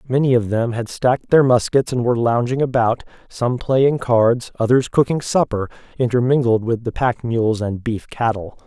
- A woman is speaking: No, male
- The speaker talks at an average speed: Yes, average, 175 wpm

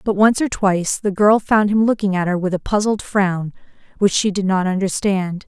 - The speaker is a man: No, female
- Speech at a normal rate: No, fast, 220 wpm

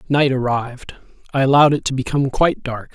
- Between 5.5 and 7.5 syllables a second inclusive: Yes, 6.6 syllables/s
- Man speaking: Yes, male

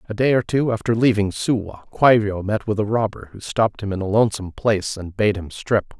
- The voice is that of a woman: No, male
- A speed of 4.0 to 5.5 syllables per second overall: No, 5.8 syllables/s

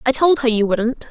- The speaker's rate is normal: No, fast, 270 wpm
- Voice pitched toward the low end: No, high, 245 Hz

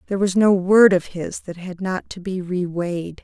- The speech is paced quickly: Yes, fast, 240 wpm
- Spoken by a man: No, female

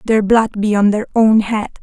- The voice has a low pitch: No, high, 215 Hz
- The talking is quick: Yes, fast, 230 wpm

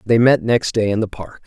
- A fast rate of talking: Yes, fast, 285 wpm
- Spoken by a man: Yes, male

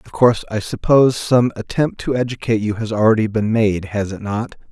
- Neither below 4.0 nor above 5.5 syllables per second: No, 5.7 syllables/s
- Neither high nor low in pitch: No, low, 110 Hz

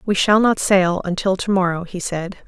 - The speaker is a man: No, female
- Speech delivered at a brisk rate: Yes, fast, 220 wpm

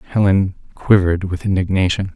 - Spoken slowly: Yes, slow, 110 wpm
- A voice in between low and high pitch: No, very low, 95 Hz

